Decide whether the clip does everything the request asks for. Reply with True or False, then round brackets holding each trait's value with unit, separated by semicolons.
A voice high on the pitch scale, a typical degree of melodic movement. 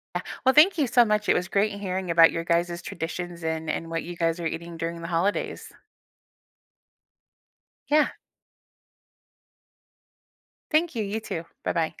False (175 Hz; 4.2 semitones)